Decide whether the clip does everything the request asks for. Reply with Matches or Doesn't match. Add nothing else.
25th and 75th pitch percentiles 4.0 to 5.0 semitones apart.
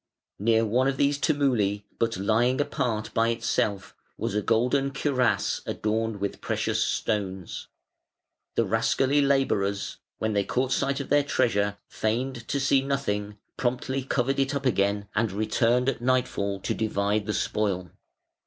Matches